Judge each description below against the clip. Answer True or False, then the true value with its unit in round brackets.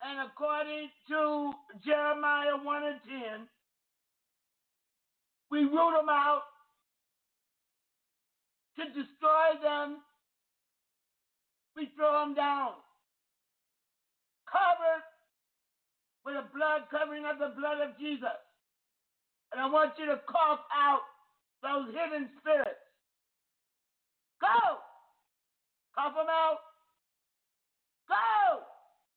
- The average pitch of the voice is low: False (295 Hz)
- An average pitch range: False (1.5 semitones)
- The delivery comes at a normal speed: False (90 wpm)